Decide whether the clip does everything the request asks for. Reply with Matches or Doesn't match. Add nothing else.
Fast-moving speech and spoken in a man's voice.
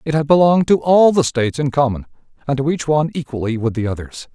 Matches